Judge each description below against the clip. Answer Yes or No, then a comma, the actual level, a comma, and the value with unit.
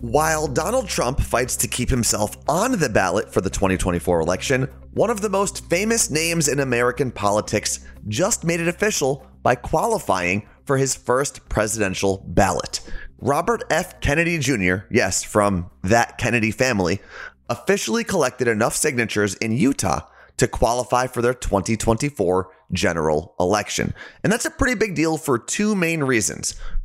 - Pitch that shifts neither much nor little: No, wide, 8.0 semitones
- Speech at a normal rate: Yes, average, 145 wpm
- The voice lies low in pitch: Yes, low, 120 Hz